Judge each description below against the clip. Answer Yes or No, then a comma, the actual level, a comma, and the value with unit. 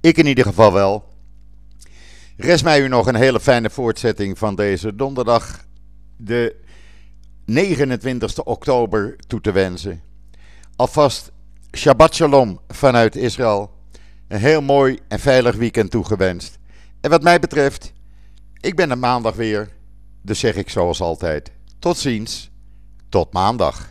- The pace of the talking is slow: Yes, slow, 130 wpm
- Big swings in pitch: Yes, wide, 6.6 semitones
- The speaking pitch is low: Yes, low, 110 Hz